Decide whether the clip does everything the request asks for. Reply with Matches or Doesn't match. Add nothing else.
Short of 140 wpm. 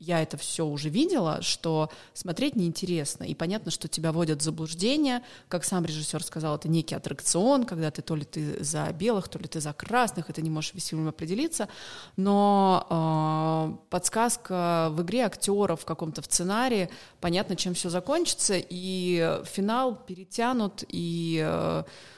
Doesn't match